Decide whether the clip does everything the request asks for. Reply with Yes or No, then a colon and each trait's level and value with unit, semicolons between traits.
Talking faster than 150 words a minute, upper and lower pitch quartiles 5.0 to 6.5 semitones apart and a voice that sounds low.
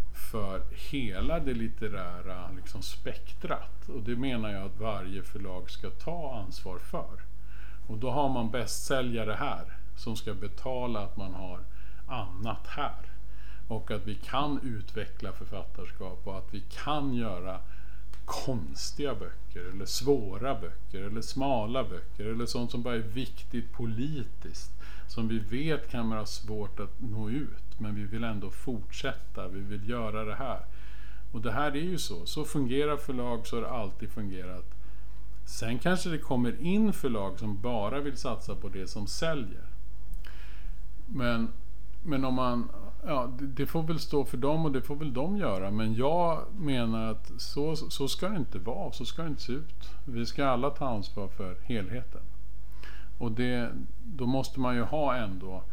Yes: average, 165 wpm; wide, 5.4 semitones; low, 115 Hz